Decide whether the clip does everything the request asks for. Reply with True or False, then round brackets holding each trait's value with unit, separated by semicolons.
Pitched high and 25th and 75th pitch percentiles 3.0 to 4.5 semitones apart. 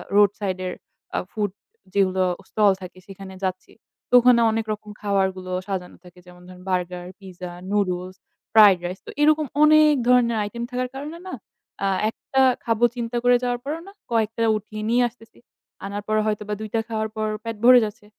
True (215 Hz; 4.1 semitones)